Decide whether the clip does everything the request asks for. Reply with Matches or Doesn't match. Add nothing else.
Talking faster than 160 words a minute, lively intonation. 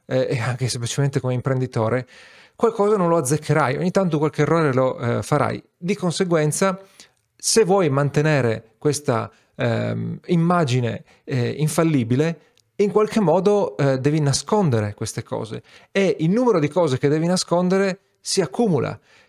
Doesn't match